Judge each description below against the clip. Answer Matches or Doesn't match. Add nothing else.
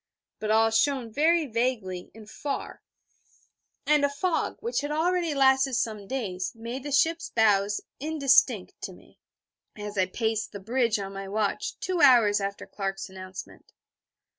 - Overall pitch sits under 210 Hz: Doesn't match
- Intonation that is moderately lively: Doesn't match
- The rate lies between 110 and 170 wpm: Matches